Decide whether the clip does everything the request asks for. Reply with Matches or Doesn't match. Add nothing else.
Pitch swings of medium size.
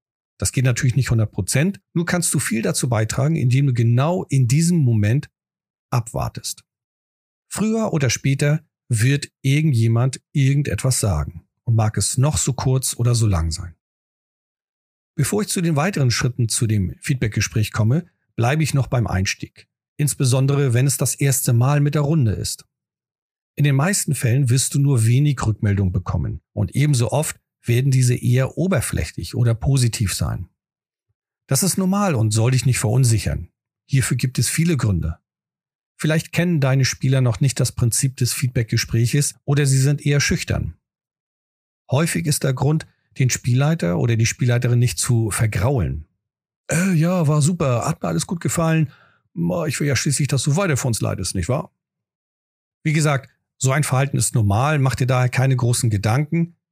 Matches